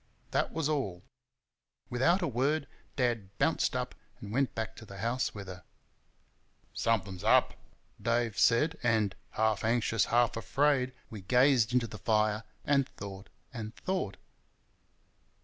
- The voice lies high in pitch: No, low, 115 Hz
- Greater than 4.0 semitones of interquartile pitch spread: No, average, 3.6 semitones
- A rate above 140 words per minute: No, slow, 135 wpm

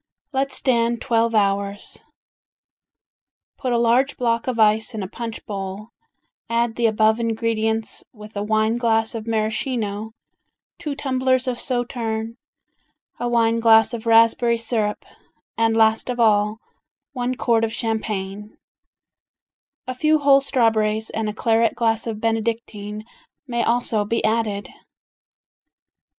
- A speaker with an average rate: No, slow, 130 wpm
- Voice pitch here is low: No, high, 225 Hz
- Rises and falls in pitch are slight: Yes, narrow, 1.7 semitones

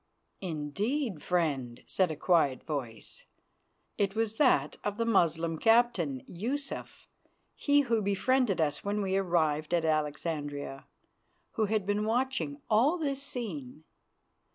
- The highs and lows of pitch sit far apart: Yes, wide, 7.1 semitones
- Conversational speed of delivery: No, slow, 125 wpm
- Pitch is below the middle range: No, high, 190 Hz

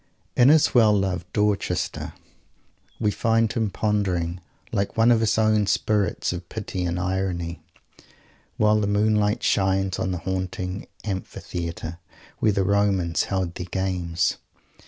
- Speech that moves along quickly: No, slow, 135 wpm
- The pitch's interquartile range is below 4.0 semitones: Yes, average, 2.9 semitones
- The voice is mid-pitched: No, very low, 95 Hz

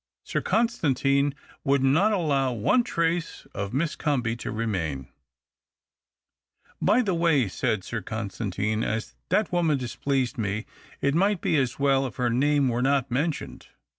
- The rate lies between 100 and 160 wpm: Yes, average, 155 wpm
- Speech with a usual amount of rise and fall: No, wide, 5.7 semitones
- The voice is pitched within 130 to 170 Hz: Yes, low, 135 Hz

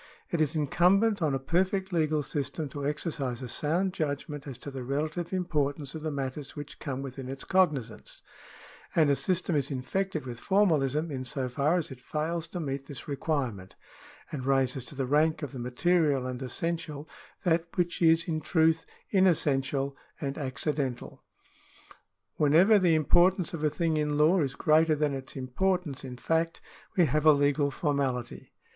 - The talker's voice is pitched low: No, medium, 150 Hz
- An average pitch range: Yes, average, 3.5 semitones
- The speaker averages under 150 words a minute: No, average, 170 wpm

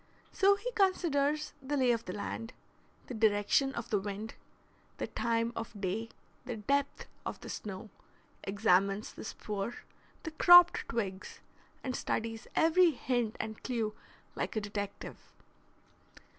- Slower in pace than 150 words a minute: Yes, slow, 135 wpm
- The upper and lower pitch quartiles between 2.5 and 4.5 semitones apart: No, average, 5.3 semitones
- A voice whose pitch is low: No, high, 230 Hz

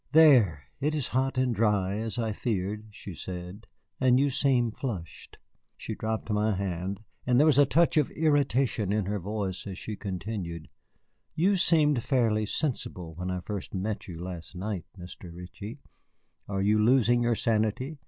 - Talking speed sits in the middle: Yes, average, 165 wpm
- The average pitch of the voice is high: No, low, 110 Hz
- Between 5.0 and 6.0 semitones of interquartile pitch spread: Yes, wide, 5.4 semitones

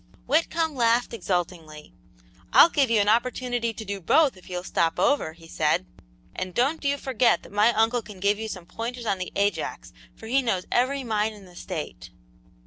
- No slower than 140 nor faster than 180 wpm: No, average, 190 wpm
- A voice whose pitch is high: Yes, high, 220 Hz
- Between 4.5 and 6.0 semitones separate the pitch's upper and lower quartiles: Yes, average, 5.1 semitones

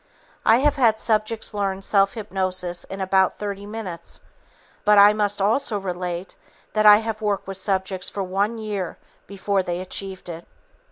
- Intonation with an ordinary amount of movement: No, narrow, 2.1 semitones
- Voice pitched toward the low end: No, high, 200 Hz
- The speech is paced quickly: No, average, 160 wpm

